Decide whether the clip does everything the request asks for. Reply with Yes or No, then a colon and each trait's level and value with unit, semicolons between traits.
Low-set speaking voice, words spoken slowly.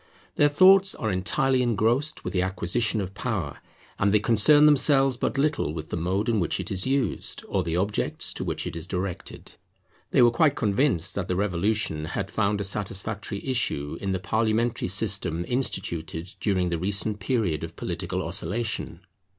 No: low, 105 Hz; average, 175 wpm